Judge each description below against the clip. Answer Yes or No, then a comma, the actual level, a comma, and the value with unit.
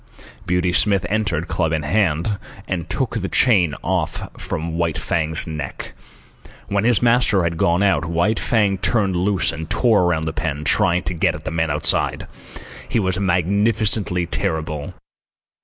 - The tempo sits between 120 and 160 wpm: Yes, average, 155 wpm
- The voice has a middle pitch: No, very low, 90 Hz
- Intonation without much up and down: No, average, 3.8 semitones